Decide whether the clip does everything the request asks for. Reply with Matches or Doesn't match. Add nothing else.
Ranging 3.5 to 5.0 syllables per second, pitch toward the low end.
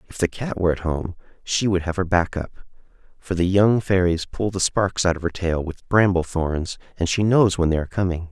Doesn't match